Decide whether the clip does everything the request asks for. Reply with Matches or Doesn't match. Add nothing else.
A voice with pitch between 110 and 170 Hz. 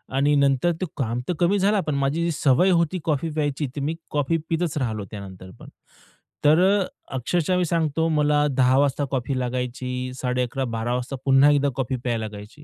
Matches